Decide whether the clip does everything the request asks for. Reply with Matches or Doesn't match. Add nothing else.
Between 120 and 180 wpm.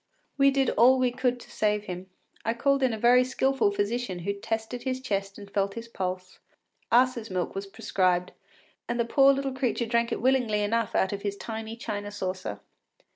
Doesn't match